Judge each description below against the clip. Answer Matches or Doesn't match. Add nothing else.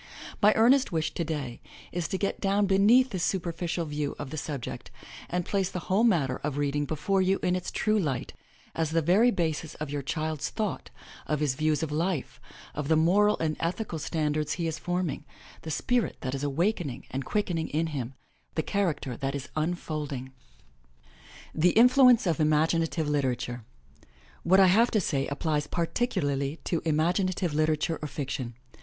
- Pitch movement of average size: Matches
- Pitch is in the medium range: Matches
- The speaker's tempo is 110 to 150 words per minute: Doesn't match